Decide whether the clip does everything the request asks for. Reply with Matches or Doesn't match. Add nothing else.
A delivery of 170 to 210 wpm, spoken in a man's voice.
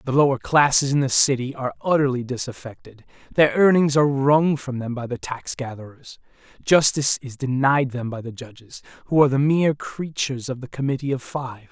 Matches